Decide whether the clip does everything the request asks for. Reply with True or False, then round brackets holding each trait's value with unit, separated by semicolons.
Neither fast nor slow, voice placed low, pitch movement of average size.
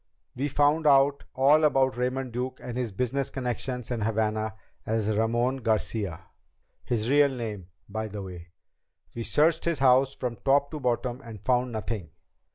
True (160 wpm; 125 Hz; 3.5 semitones)